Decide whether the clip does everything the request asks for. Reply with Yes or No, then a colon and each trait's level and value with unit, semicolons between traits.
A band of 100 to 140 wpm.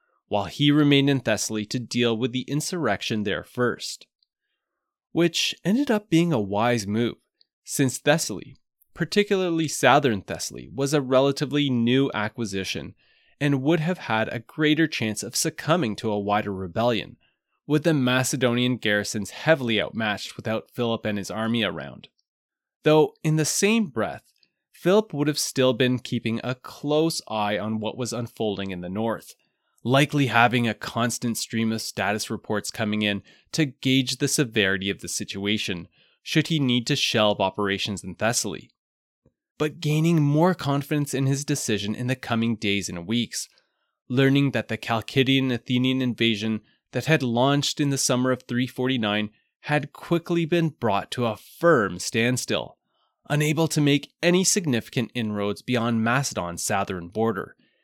No: average, 150 wpm